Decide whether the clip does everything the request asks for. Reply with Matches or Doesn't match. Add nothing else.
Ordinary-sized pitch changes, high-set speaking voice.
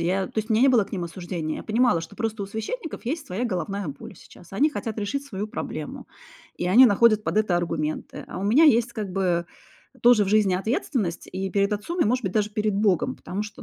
Matches